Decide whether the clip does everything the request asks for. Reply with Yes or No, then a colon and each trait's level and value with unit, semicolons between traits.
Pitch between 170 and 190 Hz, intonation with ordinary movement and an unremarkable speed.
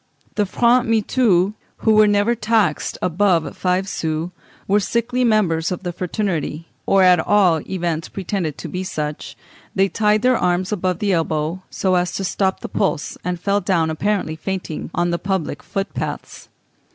Yes: medium, 185 Hz; average, 3.4 semitones; average, 165 wpm